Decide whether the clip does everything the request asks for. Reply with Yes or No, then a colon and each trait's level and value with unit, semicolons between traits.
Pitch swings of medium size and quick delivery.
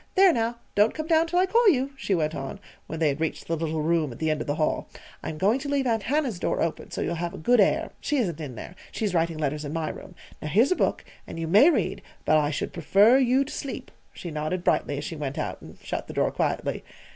No: wide, 9.0 semitones; fast, 260 wpm